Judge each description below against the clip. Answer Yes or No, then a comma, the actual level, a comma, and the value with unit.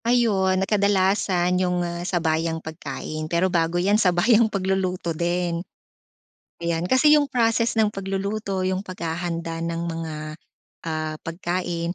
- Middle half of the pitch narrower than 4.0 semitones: Yes, average, 2.8 semitones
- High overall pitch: No, medium, 180 Hz